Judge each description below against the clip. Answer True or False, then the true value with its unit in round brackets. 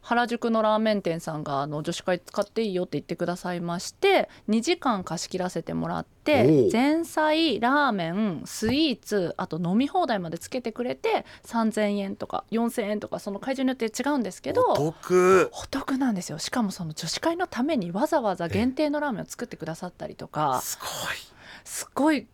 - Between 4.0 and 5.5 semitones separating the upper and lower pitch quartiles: False (6.9 semitones)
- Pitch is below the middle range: False (220 Hz)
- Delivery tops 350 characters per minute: True (375 characters per minute)